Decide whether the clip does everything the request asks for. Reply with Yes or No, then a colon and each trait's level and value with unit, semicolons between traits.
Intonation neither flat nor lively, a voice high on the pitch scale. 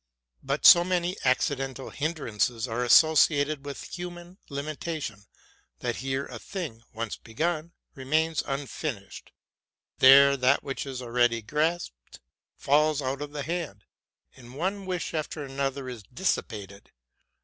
No: average, 4.2 semitones; medium, 140 Hz